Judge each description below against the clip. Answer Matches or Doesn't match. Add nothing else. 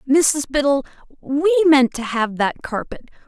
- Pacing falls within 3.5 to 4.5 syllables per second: Matches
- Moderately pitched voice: Doesn't match